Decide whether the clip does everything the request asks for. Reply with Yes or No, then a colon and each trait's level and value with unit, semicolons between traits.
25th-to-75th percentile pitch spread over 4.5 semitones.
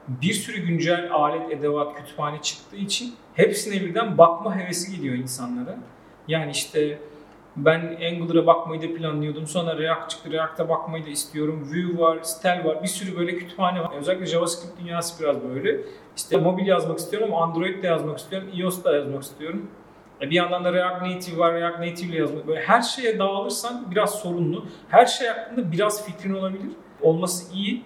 No: average, 3.2 semitones